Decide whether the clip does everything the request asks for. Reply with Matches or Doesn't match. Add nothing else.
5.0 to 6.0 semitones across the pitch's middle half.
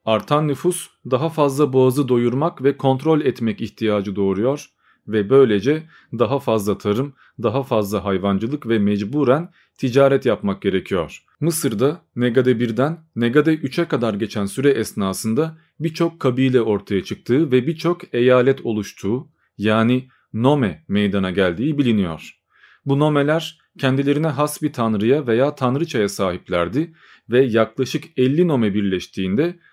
Matches